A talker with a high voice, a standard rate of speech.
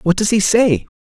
No: high, 195 Hz; fast, 235 wpm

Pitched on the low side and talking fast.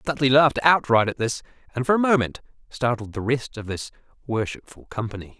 No: low, 125 Hz; average, 180 wpm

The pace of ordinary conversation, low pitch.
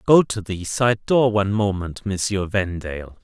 Yes: average, 165 wpm; low, 100 Hz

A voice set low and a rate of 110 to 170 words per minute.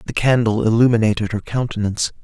Yes: low, 110 Hz; slow, 135 wpm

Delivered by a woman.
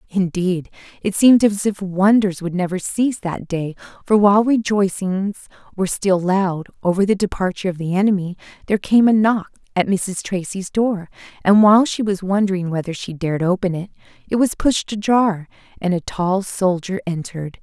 Yes: female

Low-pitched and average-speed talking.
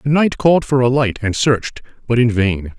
No: low, 125 Hz; fast, 235 wpm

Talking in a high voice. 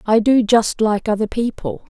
Yes: high, 215 Hz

